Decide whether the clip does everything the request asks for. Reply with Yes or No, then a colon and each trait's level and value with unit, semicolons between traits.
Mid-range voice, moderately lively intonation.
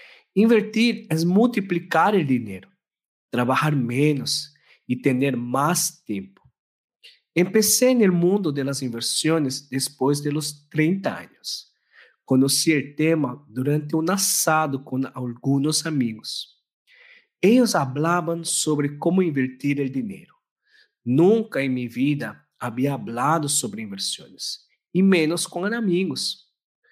No: medium, 155 Hz; wide, 5.8 semitones